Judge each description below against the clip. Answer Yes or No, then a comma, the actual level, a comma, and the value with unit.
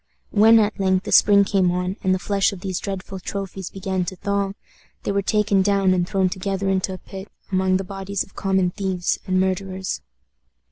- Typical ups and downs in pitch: No, narrow, 1.1 semitones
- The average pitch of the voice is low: No, high, 190 Hz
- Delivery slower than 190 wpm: No, average, 195 wpm